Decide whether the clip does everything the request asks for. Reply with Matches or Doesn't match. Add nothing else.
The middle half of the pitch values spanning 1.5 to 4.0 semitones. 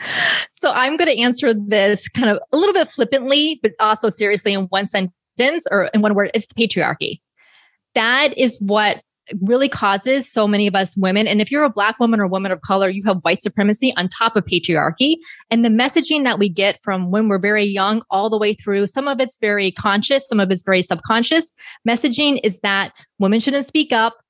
Doesn't match